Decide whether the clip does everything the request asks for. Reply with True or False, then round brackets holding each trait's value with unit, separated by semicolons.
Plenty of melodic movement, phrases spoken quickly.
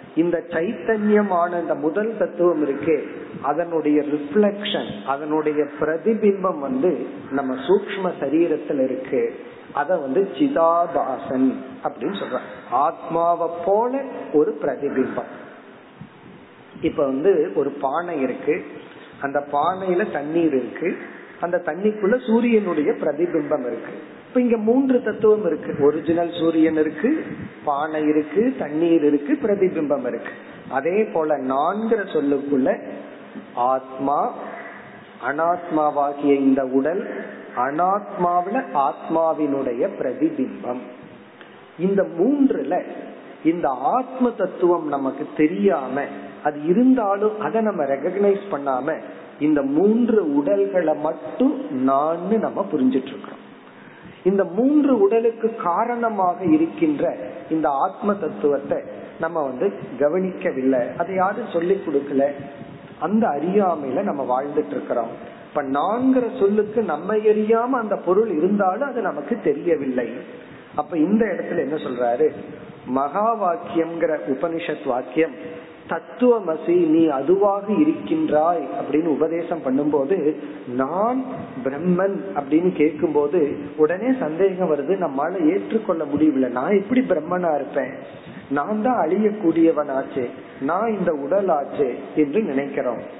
False (6.3 semitones; 95 wpm)